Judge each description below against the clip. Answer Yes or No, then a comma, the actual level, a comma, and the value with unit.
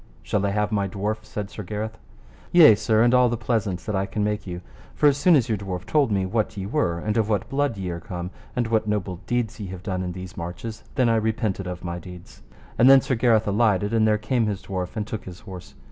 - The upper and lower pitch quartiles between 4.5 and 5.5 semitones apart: No, average, 3.3 semitones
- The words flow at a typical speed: No, fast, 255 wpm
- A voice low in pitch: Yes, low, 105 Hz